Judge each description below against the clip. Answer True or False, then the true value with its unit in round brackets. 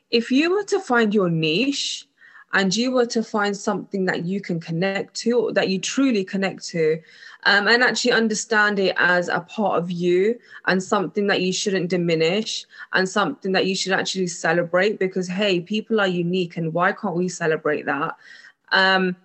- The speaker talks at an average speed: True (185 wpm)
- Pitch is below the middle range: False (195 Hz)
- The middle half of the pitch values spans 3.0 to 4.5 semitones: True (3.3 semitones)